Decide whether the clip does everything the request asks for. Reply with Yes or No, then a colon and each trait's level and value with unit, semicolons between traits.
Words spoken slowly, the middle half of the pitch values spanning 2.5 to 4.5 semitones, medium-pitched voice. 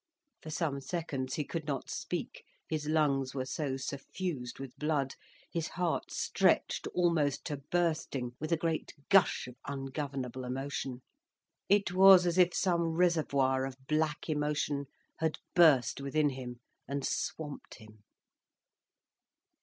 Yes: slow, 130 wpm; average, 3.6 semitones; medium, 150 Hz